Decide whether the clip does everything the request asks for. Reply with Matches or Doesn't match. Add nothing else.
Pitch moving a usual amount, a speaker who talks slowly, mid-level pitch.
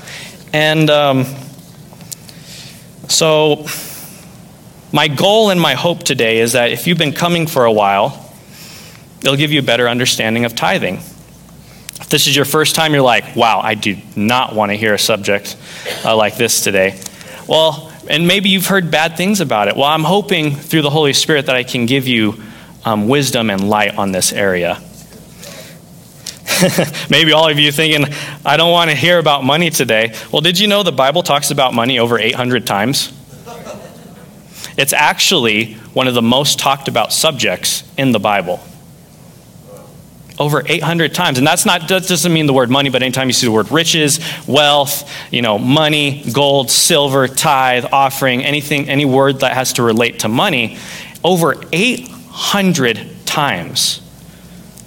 Doesn't match